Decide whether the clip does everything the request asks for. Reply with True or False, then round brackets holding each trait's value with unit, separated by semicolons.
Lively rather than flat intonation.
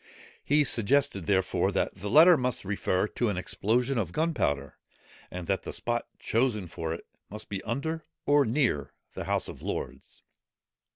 True (6.6 semitones)